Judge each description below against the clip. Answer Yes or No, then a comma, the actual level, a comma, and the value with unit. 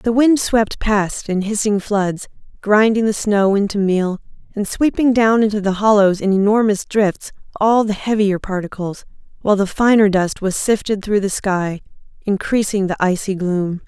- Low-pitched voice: No, high, 205 Hz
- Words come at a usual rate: Yes, average, 165 wpm